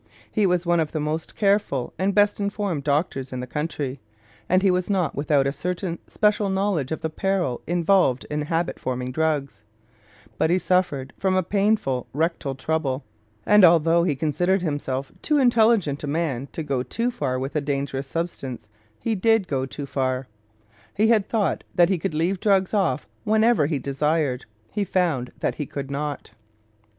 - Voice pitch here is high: No, medium, 160 Hz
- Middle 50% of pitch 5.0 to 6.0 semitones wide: Yes, wide, 5.6 semitones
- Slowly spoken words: No, average, 175 wpm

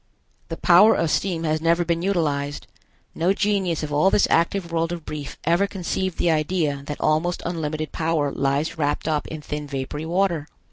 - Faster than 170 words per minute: Yes, average, 180 wpm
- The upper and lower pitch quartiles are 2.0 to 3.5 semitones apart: Yes, average, 2.7 semitones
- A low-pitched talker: No, medium, 165 Hz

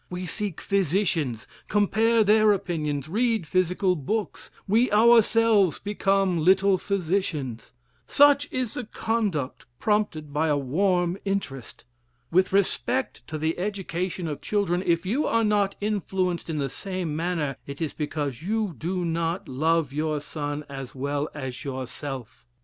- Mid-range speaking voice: Yes, medium, 180 Hz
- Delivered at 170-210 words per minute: No, average, 140 wpm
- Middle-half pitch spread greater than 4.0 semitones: Yes, average, 5.3 semitones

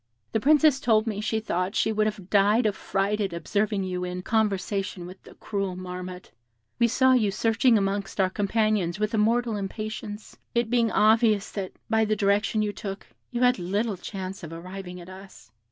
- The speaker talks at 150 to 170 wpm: No, average, 185 wpm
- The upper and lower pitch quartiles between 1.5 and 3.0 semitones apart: Yes, average, 2.7 semitones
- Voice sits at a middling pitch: No, high, 205 Hz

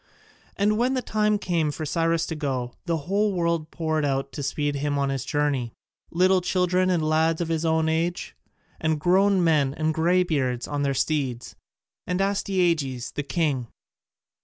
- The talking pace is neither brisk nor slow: Yes, average, 165 wpm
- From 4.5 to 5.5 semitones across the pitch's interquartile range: No, average, 3.9 semitones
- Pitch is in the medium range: Yes, medium, 160 Hz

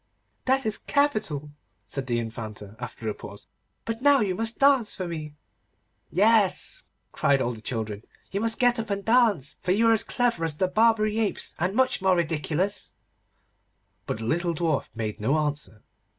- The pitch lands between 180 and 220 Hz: Yes, medium, 185 Hz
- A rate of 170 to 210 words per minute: Yes, average, 175 wpm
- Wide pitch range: Yes, wide, 8.2 semitones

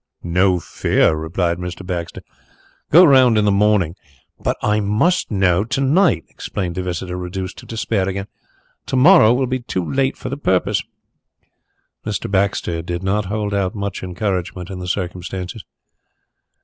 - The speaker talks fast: No, average, 160 wpm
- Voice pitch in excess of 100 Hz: No, very low, 95 Hz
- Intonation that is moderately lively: Yes, average, 3.3 semitones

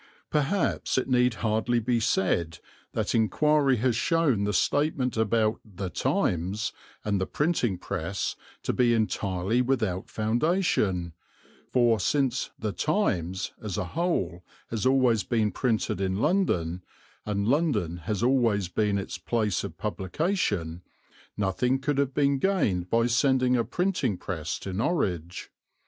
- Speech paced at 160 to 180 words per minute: No, slow, 135 wpm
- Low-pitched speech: Yes, low, 110 Hz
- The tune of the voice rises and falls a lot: Yes, wide, 5.7 semitones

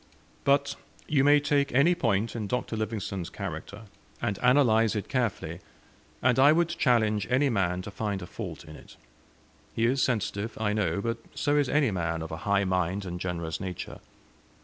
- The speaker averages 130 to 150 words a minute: No, average, 175 wpm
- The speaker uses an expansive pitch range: Yes, wide, 5.7 semitones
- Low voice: Yes, low, 110 Hz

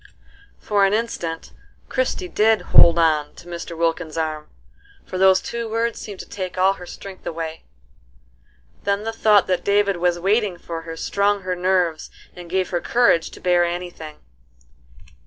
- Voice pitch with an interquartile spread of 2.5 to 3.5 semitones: Yes, average, 3.2 semitones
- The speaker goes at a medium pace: Yes, average, 170 wpm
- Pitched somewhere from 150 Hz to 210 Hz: Yes, medium, 185 Hz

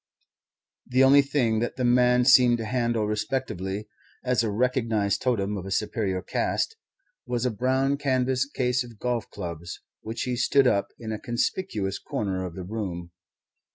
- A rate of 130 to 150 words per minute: No, average, 160 wpm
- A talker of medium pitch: No, low, 120 Hz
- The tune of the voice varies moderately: Yes, average, 3.8 semitones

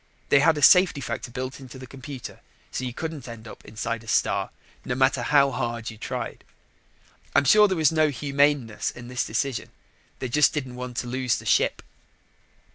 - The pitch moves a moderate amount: Yes, average, 3.1 semitones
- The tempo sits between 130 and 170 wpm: No, average, 190 wpm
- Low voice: Yes, low, 130 Hz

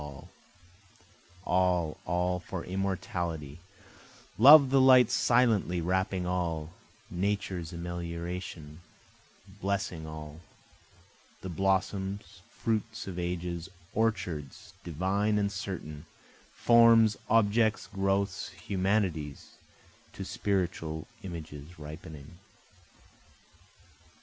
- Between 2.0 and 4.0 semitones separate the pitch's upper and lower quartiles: Yes, average, 3.3 semitones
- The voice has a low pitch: Yes, very low, 90 Hz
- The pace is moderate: No, slow, 80 wpm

